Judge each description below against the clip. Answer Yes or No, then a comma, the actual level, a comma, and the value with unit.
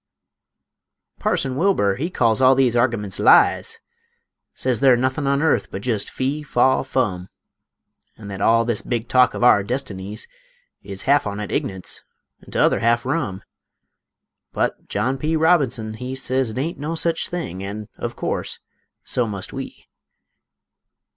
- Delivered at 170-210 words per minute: No, average, 150 wpm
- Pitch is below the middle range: Yes, low, 125 Hz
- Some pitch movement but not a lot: Yes, average, 4.3 semitones